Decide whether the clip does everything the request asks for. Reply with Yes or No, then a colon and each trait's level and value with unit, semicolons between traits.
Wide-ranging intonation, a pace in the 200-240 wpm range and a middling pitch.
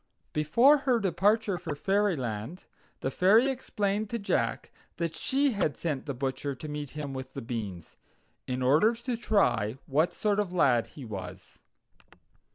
No: wide, 8.0 semitones; average, 155 wpm; medium, 160 Hz